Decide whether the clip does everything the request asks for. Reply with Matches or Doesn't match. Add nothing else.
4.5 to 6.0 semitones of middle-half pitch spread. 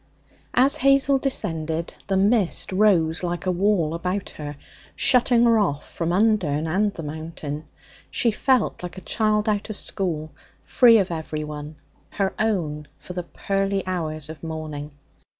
Matches